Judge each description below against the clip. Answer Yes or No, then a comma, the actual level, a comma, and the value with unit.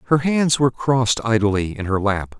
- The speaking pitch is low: Yes, low, 120 Hz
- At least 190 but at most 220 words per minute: Yes, average, 200 wpm